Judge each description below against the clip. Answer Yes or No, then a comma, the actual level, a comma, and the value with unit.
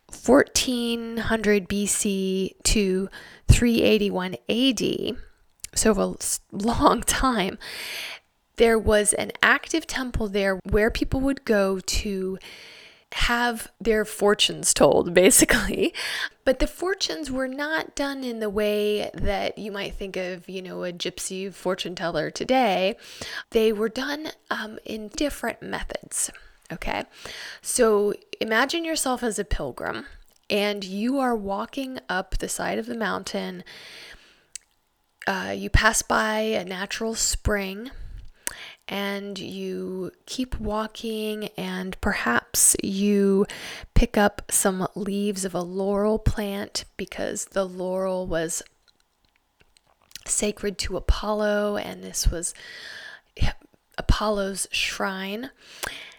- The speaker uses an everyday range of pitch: Yes, average, 3.4 semitones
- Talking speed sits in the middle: No, slow, 110 wpm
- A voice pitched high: Yes, high, 210 Hz